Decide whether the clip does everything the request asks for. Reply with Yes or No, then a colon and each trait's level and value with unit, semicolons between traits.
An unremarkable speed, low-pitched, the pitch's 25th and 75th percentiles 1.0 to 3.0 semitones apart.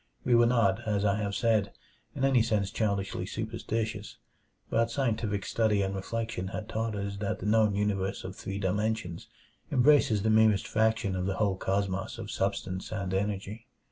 Yes: average, 170 wpm; low, 105 Hz; narrow, 2.4 semitones